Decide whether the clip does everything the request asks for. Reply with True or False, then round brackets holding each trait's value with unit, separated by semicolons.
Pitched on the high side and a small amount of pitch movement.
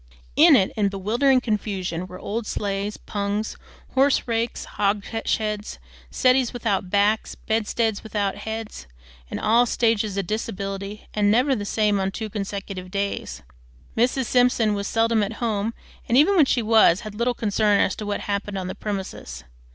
True (210 Hz; 2.3 semitones)